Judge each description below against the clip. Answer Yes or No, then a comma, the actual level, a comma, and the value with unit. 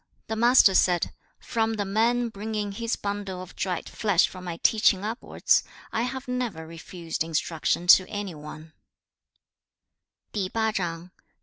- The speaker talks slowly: Yes, slow, 125 wpm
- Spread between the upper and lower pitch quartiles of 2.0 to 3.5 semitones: No, average, 4.2 semitones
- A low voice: No, high, 200 Hz